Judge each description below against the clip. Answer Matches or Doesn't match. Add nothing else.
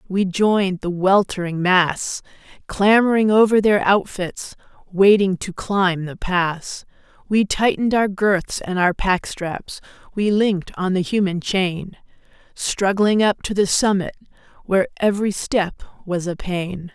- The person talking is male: Doesn't match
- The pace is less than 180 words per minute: Matches